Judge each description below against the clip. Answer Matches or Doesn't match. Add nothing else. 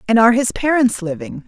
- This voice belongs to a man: Doesn't match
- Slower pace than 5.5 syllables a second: Doesn't match